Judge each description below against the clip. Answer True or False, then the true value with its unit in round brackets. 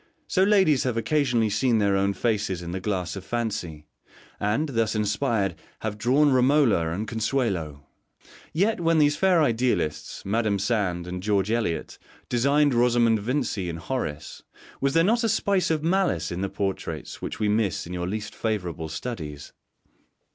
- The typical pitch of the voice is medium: False (110 Hz)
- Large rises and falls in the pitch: True (6.1 semitones)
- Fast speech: False (160 wpm)